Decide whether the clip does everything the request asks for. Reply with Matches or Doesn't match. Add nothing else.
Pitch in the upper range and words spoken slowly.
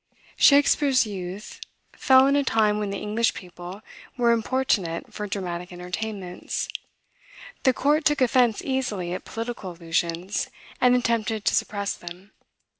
Matches